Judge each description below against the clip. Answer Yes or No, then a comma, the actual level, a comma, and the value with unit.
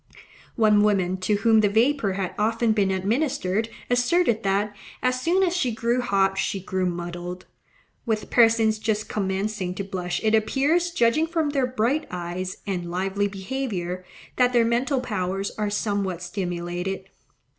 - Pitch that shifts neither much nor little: Yes, average, 4.3 semitones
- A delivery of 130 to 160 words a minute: Yes, average, 150 wpm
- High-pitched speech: Yes, high, 210 Hz